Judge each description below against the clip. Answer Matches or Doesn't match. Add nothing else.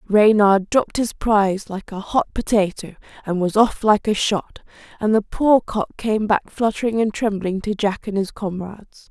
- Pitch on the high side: Matches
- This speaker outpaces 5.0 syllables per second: Doesn't match